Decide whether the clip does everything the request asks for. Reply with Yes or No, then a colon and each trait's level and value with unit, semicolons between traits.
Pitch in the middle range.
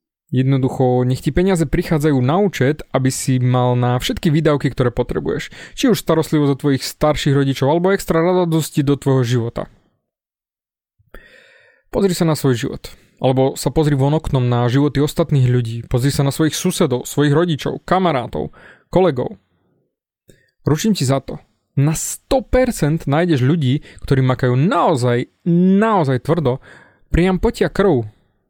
Yes: medium, 145 Hz